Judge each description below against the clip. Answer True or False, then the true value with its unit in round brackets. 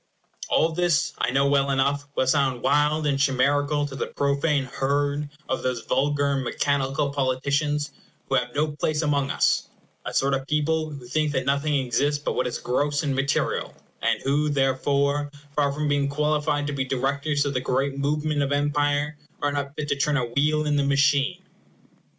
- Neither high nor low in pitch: True (145 Hz)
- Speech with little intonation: True (1.3 semitones)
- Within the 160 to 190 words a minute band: True (185 wpm)